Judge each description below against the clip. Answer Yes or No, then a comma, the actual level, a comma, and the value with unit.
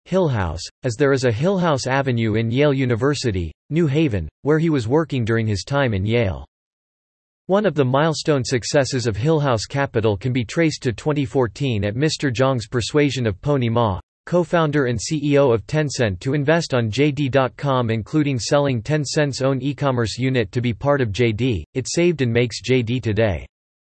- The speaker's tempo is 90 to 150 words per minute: No, average, 175 wpm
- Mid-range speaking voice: No, low, 130 Hz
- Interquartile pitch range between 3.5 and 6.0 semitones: Yes, average, 3.9 semitones